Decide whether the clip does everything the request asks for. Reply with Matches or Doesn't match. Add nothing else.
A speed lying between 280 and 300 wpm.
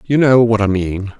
Doesn't match